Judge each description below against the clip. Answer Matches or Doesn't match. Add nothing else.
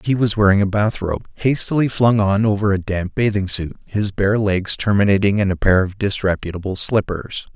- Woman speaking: Doesn't match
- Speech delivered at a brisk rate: Doesn't match